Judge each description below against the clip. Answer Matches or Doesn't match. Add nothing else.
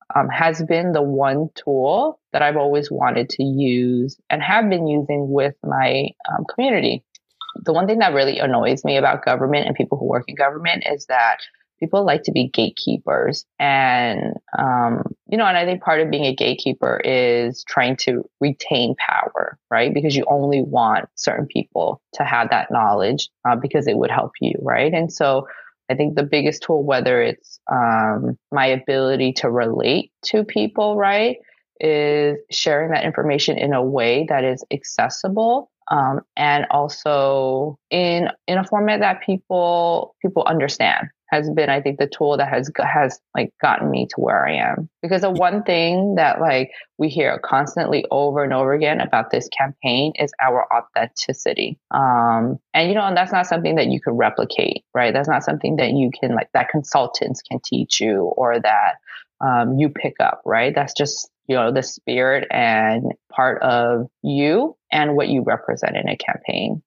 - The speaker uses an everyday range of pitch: Matches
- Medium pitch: Matches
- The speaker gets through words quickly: Doesn't match